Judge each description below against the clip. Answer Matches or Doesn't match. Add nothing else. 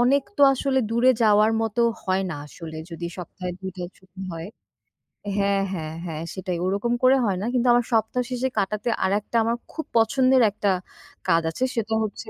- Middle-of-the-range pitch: Doesn't match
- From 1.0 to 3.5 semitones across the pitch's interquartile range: Doesn't match